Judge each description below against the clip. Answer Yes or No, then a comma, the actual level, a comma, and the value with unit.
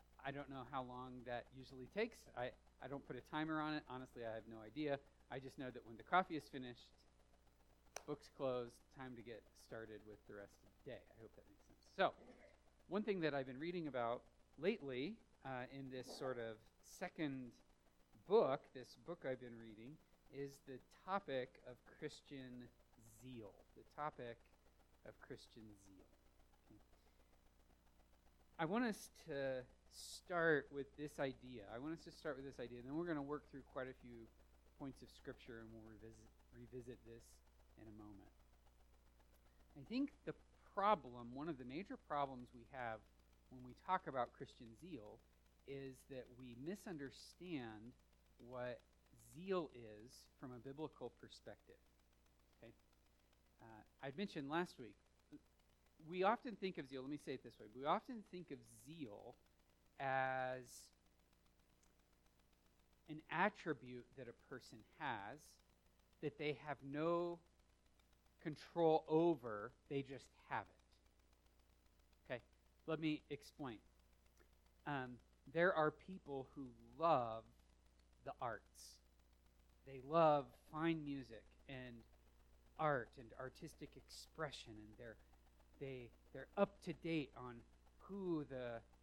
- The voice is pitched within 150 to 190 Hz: No, low, 125 Hz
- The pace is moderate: Yes, average, 145 wpm